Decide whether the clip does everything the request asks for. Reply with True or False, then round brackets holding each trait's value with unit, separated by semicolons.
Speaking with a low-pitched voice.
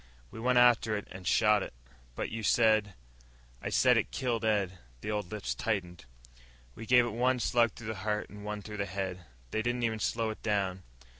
True (105 Hz)